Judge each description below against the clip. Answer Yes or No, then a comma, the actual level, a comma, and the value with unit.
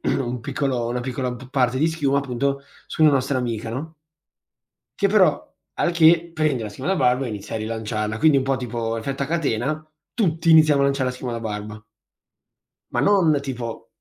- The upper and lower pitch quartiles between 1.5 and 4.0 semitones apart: No, average, 4.6 semitones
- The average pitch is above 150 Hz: No, low, 135 Hz